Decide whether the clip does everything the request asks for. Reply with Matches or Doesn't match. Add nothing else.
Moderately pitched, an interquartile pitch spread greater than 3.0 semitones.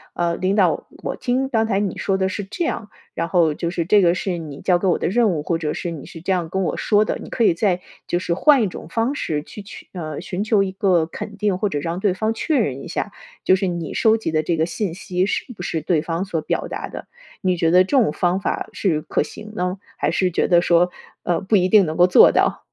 Matches